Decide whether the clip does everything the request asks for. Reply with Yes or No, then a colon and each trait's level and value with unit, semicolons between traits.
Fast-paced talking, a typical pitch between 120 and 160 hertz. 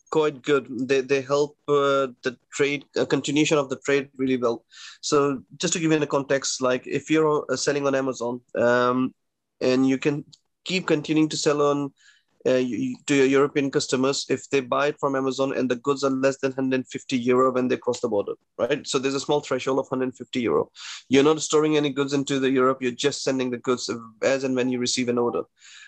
Yes: fast, 215 wpm; medium, 140 Hz